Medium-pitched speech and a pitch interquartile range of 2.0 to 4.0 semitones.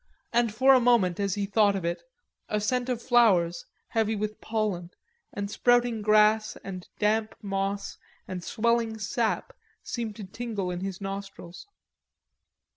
No: high, 210 Hz; average, 2.7 semitones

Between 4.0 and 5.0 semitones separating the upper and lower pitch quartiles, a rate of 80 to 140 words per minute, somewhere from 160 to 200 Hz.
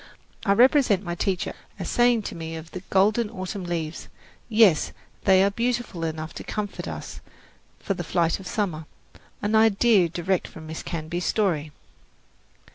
No: average, 4.3 semitones; average, 155 wpm; high, 190 Hz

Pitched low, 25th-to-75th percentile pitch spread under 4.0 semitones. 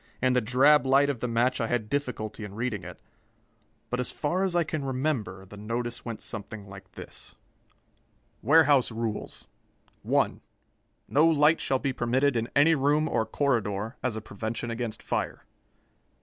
No: low, 125 Hz; average, 4.3 semitones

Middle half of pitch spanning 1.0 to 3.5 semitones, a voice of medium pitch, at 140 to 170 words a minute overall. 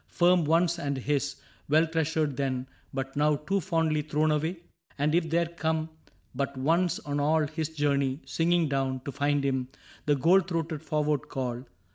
Yes: narrow, 2.6 semitones; medium, 150 Hz; average, 165 wpm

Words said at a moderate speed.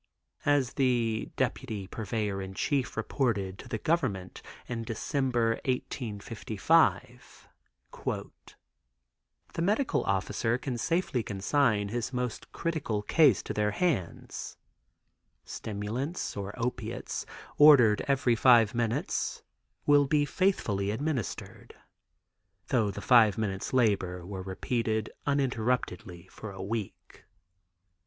No: slow, 105 wpm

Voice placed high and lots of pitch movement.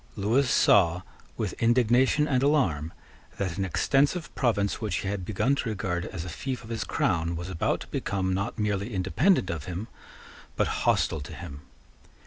No: low, 100 Hz; wide, 5.7 semitones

